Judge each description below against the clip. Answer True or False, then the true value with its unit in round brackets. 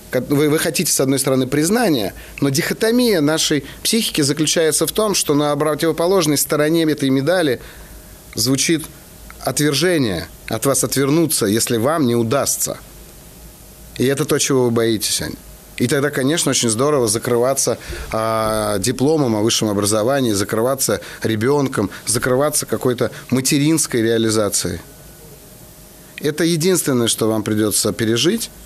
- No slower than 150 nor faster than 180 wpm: False (120 wpm)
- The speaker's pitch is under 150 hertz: True (140 Hz)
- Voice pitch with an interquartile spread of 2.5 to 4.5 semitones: False (5.1 semitones)